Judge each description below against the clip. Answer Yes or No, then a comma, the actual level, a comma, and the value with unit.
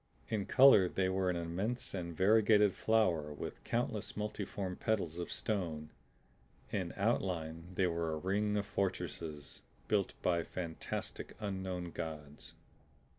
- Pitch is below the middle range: Yes, very low, 95 Hz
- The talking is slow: Yes, slow, 125 wpm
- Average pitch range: Yes, average, 3.8 semitones